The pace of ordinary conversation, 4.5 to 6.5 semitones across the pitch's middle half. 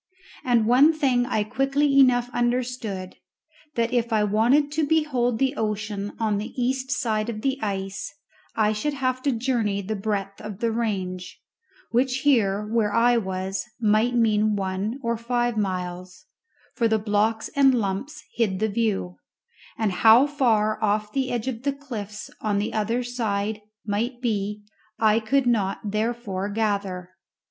No: average, 155 wpm; average, 3.2 semitones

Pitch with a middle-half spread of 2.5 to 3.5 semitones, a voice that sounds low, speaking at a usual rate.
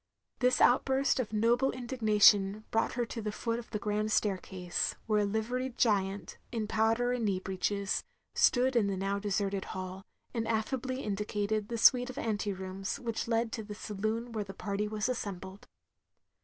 No: average, 3.0 semitones; high, 215 Hz; average, 170 wpm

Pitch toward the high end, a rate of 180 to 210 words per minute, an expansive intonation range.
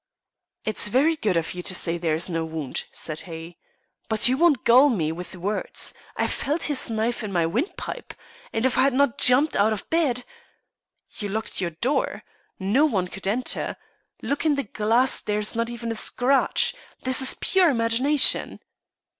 Yes: high, 230 Hz; average, 185 wpm; wide, 6.0 semitones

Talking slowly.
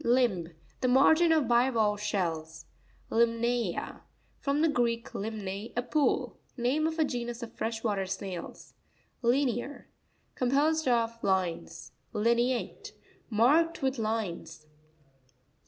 Yes: slow, 100 wpm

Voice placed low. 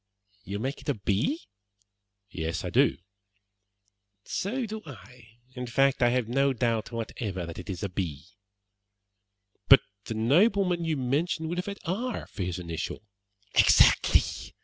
Yes: low, 125 Hz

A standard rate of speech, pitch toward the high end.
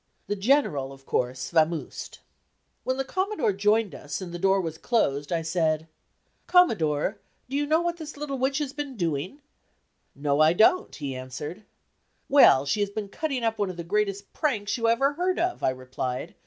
Yes: average, 180 wpm; high, 200 Hz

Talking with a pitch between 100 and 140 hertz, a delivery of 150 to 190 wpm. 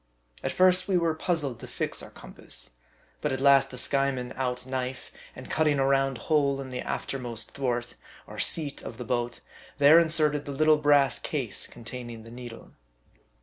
Yes: low, 135 Hz; average, 180 wpm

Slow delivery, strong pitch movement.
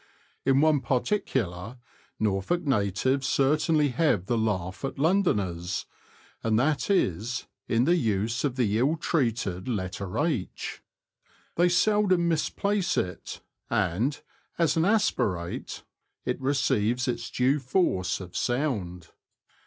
Yes: slow, 115 wpm; wide, 7.5 semitones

